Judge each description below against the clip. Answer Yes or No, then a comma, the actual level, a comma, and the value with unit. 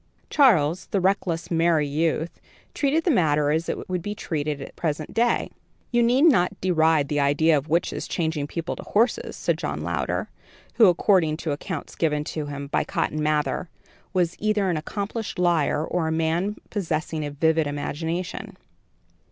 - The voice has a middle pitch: Yes, medium, 165 Hz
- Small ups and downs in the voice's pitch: No, average, 3.7 semitones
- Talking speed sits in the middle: Yes, average, 170 wpm